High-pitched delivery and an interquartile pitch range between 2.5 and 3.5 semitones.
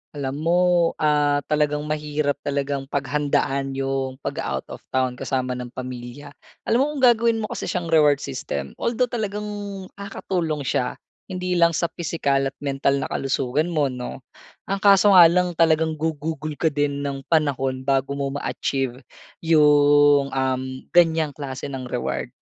No: medium, 145 Hz; average, 3.2 semitones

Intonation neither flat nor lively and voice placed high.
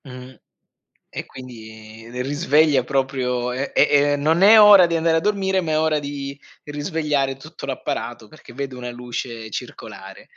No: average, 4.1 semitones; medium, 140 Hz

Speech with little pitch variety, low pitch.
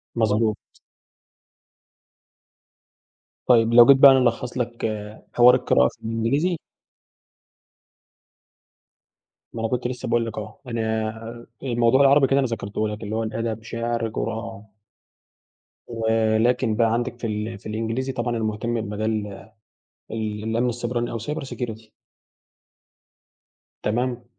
Yes: narrow, 1.6 semitones; low, 115 Hz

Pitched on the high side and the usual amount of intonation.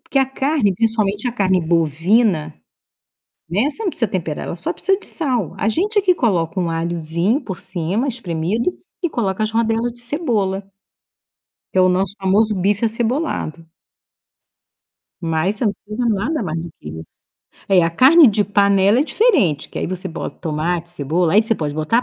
No: high, 200 Hz; wide, 5.8 semitones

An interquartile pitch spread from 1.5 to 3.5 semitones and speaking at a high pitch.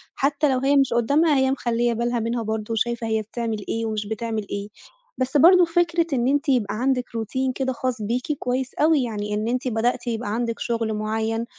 Yes: average, 3.0 semitones; high, 240 Hz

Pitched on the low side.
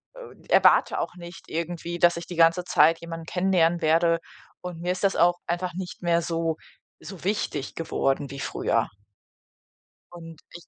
No: medium, 170 Hz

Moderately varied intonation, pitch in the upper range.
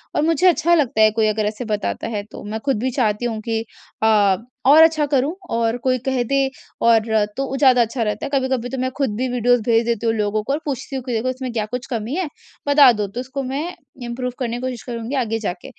Yes: average, 3.3 semitones; high, 245 Hz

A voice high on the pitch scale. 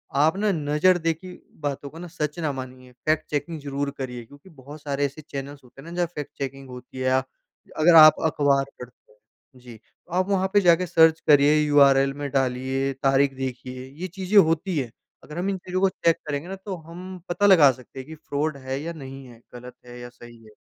No: medium, 145 Hz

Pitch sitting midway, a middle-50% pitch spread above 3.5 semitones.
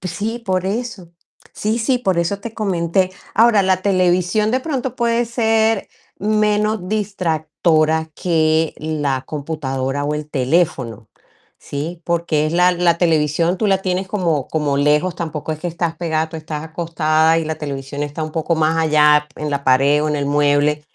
Yes: medium, 165 Hz; average, 4.2 semitones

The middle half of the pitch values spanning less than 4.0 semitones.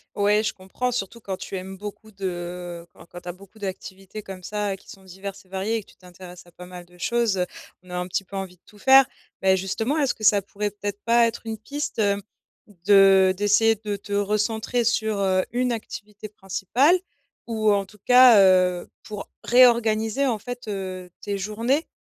Yes: average, 2.7 semitones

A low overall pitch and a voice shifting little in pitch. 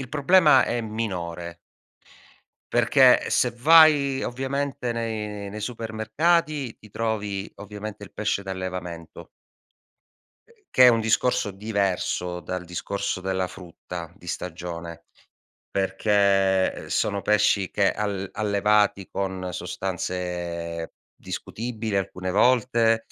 No: low, 100 Hz; average, 3.8 semitones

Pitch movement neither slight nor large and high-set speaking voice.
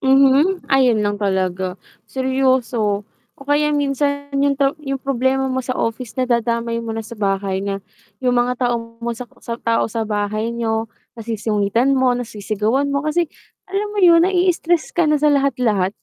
Yes: average, 4.0 semitones; high, 245 Hz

